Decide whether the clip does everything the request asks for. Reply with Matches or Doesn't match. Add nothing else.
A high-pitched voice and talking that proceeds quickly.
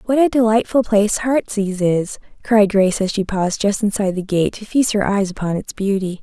Matches